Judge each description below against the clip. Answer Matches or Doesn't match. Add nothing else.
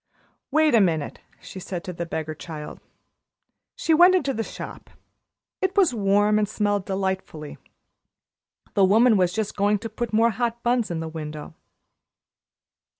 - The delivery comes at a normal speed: Matches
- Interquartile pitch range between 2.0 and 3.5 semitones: Doesn't match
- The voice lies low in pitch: Doesn't match